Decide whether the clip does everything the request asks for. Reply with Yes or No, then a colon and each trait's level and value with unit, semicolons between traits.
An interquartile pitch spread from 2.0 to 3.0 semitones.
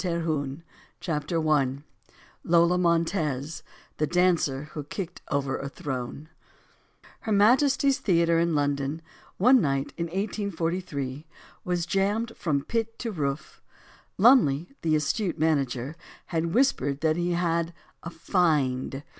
No: average, 4.1 semitones